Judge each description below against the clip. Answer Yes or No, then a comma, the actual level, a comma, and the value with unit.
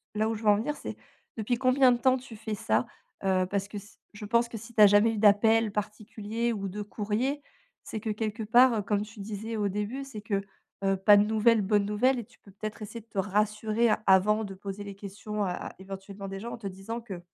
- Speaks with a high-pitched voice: Yes, high, 210 Hz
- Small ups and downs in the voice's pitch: Yes, narrow, 2.1 semitones